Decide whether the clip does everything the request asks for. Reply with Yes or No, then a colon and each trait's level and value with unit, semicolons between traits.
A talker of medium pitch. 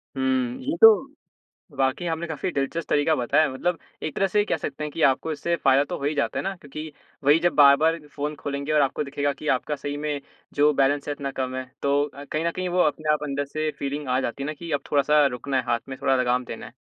Yes: medium, 145 Hz